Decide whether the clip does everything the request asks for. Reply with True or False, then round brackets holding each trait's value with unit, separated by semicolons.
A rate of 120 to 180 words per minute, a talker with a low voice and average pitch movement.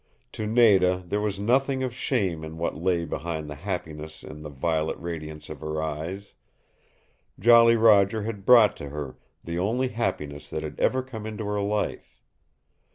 False (165 wpm; 95 Hz; 5.8 semitones)